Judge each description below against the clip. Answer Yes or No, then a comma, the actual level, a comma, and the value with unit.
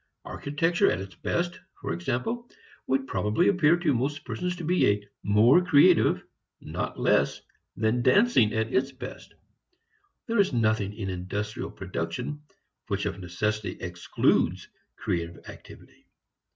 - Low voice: Yes, low, 125 Hz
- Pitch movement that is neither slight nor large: No, wide, 8.3 semitones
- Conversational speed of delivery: No, slow, 125 wpm